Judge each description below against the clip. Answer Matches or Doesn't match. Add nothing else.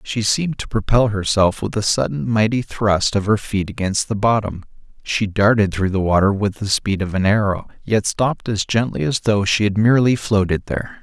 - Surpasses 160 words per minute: Matches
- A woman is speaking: Doesn't match